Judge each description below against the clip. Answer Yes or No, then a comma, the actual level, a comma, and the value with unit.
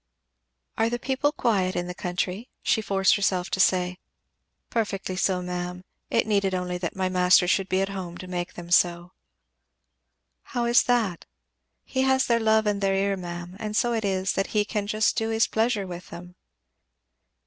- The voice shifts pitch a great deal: No, average, 3.4 semitones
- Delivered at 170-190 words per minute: Yes, average, 180 wpm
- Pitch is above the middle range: Yes, high, 195 Hz